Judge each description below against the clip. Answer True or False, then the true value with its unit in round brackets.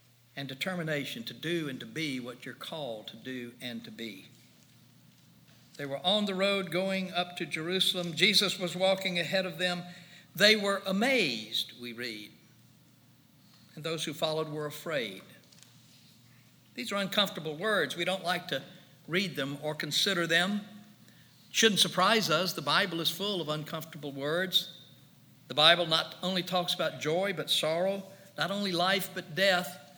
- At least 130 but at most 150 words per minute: False (160 wpm)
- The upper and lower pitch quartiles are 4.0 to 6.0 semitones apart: True (5.2 semitones)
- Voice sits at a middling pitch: True (165 Hz)